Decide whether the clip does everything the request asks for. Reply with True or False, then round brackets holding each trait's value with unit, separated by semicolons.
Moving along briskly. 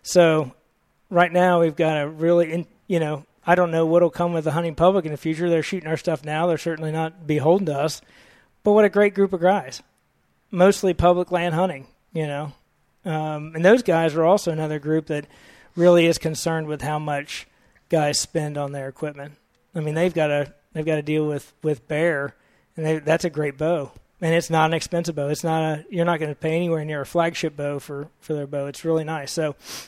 True (220 wpm)